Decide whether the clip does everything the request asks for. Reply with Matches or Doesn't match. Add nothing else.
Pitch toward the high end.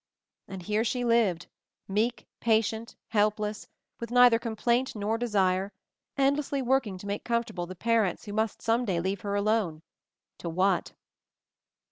Matches